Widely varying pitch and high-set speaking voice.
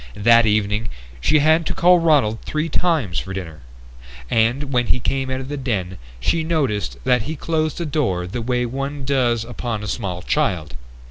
No: wide, 5.7 semitones; low, 125 Hz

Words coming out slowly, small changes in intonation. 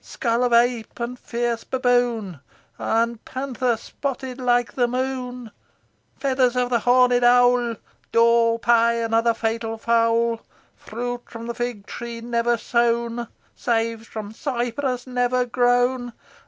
Yes: slow, 125 wpm; narrow, 1.2 semitones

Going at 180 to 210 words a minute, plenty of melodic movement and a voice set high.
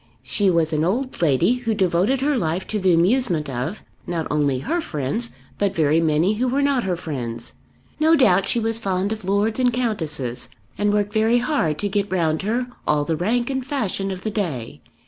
Yes: average, 200 wpm; wide, 6.6 semitones; high, 195 Hz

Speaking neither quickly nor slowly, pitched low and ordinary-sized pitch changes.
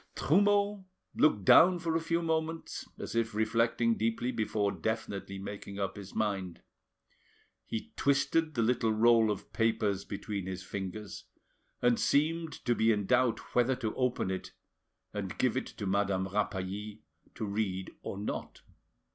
Yes: average, 145 wpm; low, 110 Hz; average, 4.2 semitones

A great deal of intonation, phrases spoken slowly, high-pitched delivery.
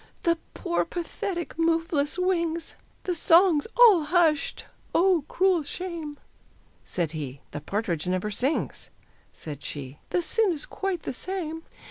Yes: wide, 5.8 semitones; slow, 130 wpm; very high, 330 Hz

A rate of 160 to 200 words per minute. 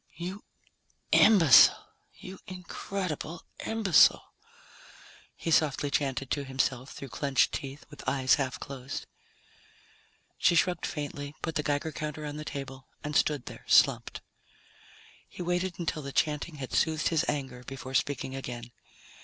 No: slow, 135 wpm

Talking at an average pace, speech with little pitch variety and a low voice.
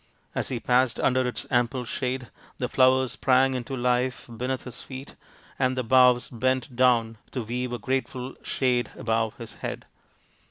Yes: average, 160 wpm; narrow, 1.2 semitones; low, 125 Hz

